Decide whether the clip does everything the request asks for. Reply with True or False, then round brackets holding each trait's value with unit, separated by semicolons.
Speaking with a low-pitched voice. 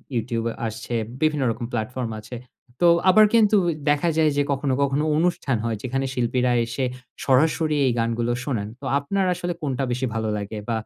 True (130 Hz)